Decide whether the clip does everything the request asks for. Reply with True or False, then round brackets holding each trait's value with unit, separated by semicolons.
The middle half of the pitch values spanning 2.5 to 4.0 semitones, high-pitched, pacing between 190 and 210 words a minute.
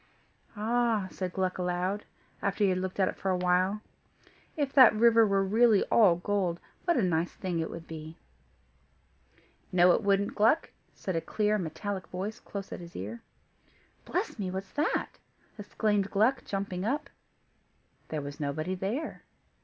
False (3.0 semitones; 195 Hz; 160 wpm)